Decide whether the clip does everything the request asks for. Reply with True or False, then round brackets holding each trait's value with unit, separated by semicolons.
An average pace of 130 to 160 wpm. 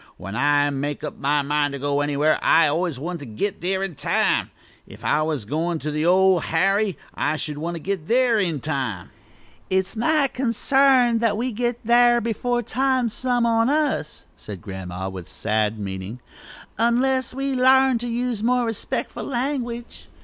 False (175 wpm)